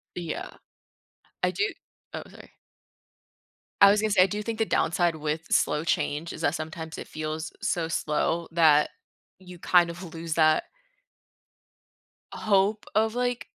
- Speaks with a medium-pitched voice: Yes, medium, 170 Hz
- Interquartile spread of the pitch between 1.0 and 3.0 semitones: No, average, 4.0 semitones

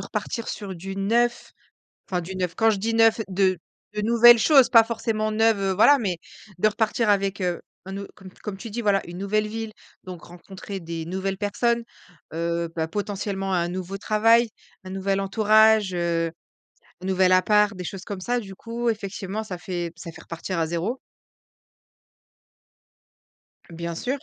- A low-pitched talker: No, high, 195 Hz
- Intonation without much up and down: No, average, 3.1 semitones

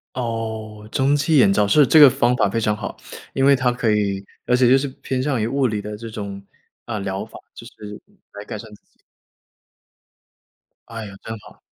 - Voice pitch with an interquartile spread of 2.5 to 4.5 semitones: Yes, average, 3.7 semitones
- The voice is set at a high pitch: No, low, 115 Hz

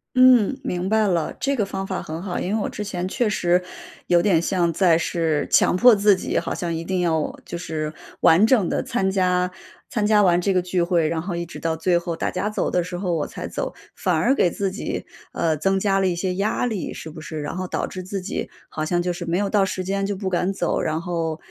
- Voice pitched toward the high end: No, medium, 180 Hz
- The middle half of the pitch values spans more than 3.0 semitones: No, narrow, 2.6 semitones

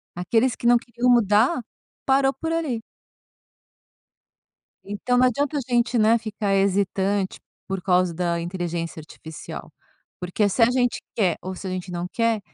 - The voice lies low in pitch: No, high, 210 Hz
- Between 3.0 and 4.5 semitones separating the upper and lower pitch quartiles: No, average, 4.9 semitones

